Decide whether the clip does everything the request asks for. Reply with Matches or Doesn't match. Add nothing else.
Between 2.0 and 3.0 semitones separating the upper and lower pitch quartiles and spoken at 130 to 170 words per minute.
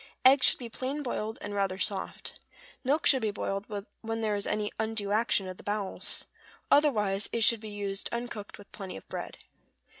Doesn't match